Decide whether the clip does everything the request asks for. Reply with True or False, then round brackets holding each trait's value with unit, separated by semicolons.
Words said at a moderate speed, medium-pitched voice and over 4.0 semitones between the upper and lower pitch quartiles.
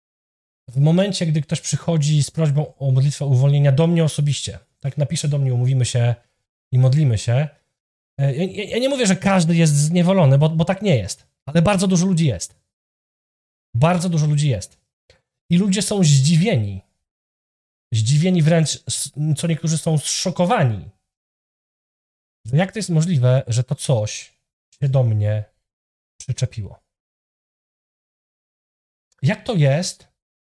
True (135 wpm; 145 Hz; 5.5 semitones)